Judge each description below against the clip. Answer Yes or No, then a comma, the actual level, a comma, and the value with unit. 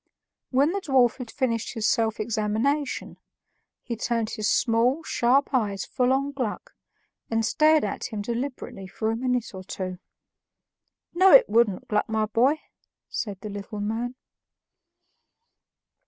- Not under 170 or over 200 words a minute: No, average, 140 wpm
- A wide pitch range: No, average, 3.6 semitones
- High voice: Yes, high, 230 Hz